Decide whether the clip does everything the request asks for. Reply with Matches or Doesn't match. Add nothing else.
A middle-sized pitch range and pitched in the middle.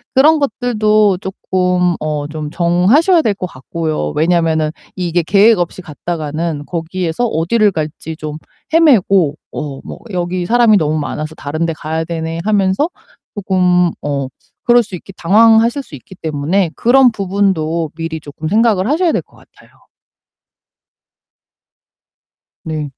Matches